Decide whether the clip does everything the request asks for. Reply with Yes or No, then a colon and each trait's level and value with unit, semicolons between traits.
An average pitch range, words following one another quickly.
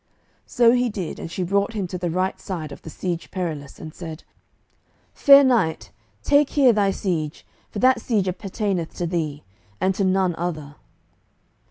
No: average, 4.3 semitones; average, 170 wpm